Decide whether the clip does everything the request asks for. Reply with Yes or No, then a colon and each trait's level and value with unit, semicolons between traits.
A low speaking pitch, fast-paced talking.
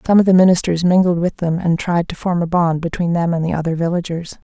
No: medium, 170 Hz; fast, 250 wpm